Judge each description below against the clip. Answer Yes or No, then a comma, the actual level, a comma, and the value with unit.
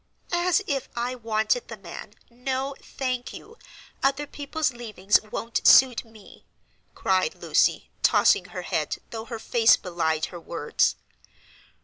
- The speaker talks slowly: Yes, slow, 130 wpm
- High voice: Yes, high, 235 Hz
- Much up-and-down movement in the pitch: No, average, 4.1 semitones